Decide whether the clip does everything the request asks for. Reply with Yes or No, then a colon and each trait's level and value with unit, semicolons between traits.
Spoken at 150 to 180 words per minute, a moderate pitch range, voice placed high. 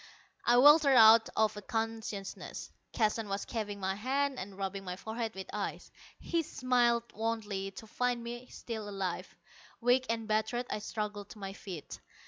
Yes: average, 155 wpm; average, 3.1 semitones; high, 220 Hz